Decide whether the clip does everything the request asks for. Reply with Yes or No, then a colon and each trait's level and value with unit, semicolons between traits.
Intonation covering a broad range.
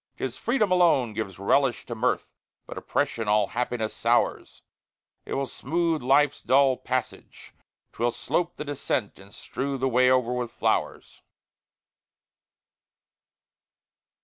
No: average, 3.2 semitones